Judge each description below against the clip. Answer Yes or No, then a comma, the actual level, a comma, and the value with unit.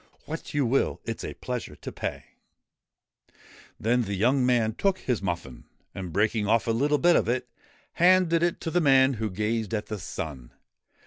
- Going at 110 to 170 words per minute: No, average, 190 wpm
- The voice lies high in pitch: No, low, 115 Hz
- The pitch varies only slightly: No, average, 5.1 semitones